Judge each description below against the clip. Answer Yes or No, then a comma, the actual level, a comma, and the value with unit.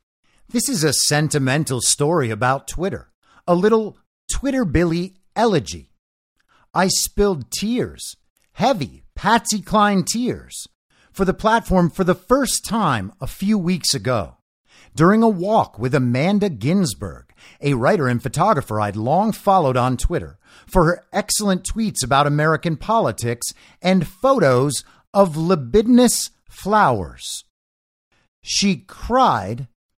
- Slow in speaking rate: Yes, slow, 120 wpm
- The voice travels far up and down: Yes, wide, 8.4 semitones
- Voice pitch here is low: No, medium, 175 Hz